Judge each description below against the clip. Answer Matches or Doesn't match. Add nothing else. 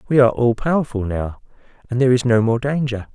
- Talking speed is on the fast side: Matches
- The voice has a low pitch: Matches